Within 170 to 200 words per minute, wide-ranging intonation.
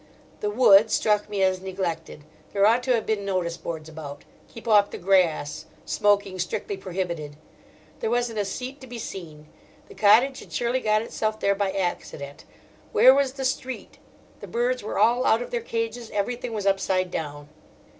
No: average, 175 wpm; average, 4.3 semitones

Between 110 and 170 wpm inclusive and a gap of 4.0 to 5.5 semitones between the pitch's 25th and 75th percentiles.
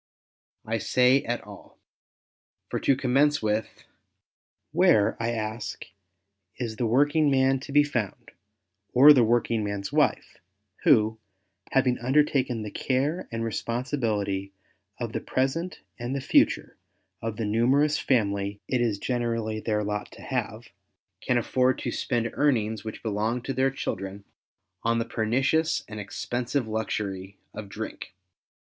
No: average, 140 wpm; average, 3.6 semitones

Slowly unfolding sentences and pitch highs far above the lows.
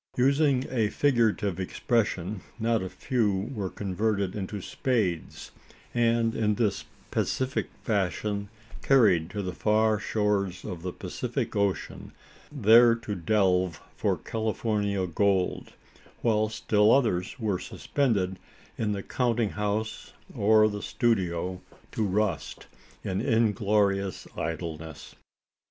No: slow, 110 wpm; average, 3.0 semitones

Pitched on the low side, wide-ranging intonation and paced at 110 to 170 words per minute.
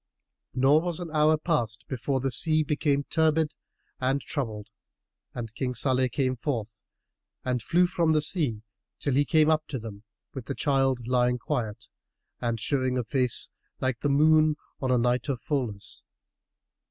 No: low, 130 Hz; average, 3.9 semitones; average, 160 wpm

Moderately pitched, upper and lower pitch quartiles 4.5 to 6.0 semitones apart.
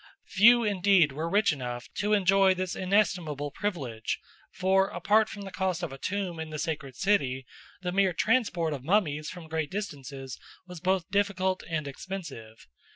Yes: medium, 180 Hz; average, 4.9 semitones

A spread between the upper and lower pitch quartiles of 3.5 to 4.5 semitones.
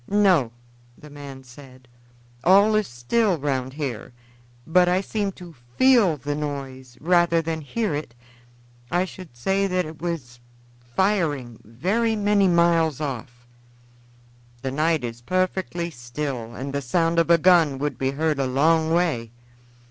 No: wide, 5.4 semitones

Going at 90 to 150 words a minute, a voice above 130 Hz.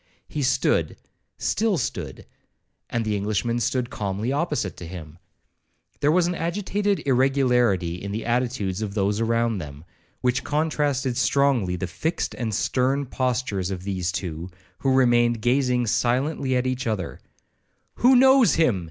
No: average, 140 wpm; low, 120 Hz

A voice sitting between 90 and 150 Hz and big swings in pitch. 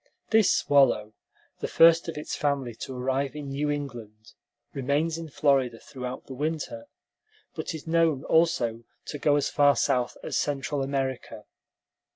No: medium, 140 Hz; average, 2.9 semitones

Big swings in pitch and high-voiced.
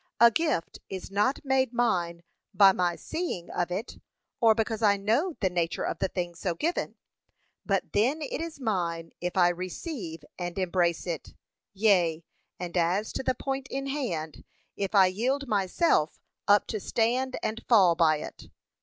Yes: wide, 6.2 semitones; high, 200 Hz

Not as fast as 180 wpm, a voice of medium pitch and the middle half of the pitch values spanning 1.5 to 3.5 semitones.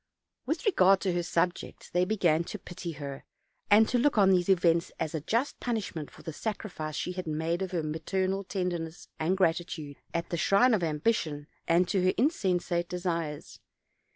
No: average, 185 wpm; medium, 175 Hz; average, 3.0 semitones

